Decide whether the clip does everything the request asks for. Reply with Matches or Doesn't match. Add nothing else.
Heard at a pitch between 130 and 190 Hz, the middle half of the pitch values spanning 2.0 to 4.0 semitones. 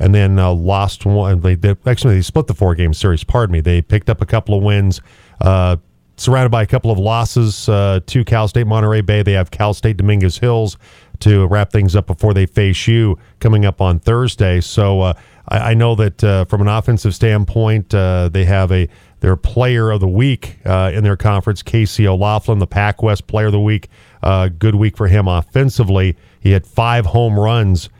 Doesn't match